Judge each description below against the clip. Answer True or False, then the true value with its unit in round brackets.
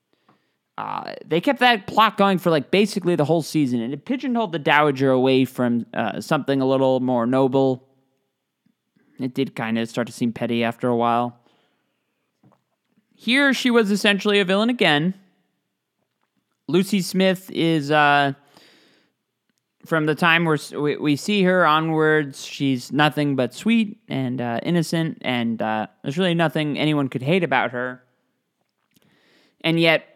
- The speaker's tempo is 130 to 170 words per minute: True (150 wpm)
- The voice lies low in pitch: False (150 Hz)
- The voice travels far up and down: True (6.4 semitones)